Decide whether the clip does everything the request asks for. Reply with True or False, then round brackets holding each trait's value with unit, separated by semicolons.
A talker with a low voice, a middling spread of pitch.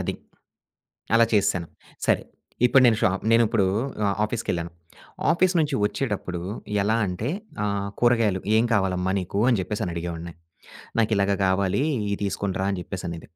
True (100 Hz; 3.7 semitones)